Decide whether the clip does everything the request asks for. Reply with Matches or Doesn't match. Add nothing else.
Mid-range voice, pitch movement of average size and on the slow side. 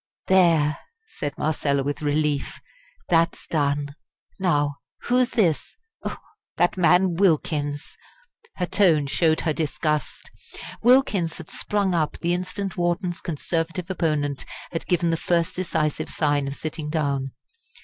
Matches